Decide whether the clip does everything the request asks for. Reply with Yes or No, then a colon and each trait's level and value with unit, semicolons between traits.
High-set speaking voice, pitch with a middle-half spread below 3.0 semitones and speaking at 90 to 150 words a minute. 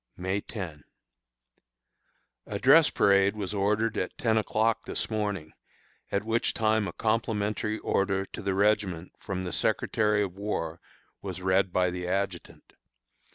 No: low, 100 Hz; narrow, 2.5 semitones; average, 140 wpm